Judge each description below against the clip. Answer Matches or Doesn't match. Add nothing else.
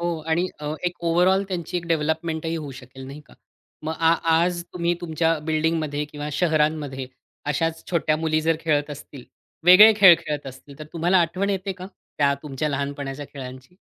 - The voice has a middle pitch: Matches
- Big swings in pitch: Doesn't match